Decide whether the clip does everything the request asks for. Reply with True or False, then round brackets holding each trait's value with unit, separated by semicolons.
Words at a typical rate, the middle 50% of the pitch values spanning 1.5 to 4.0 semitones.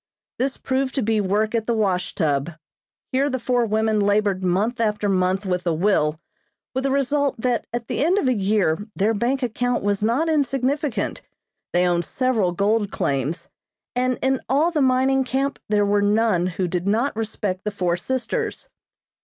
False (180 wpm; 5.2 semitones)